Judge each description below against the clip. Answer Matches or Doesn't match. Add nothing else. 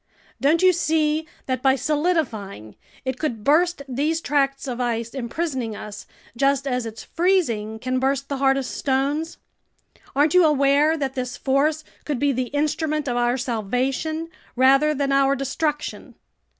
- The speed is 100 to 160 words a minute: Matches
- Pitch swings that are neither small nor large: Matches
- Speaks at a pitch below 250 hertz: Doesn't match